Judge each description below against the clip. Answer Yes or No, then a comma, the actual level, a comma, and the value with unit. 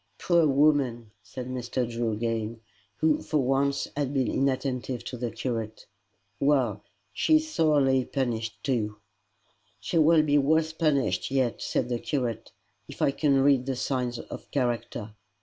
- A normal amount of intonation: Yes, average, 3.3 semitones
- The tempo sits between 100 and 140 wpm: No, average, 150 wpm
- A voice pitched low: Yes, low, 130 Hz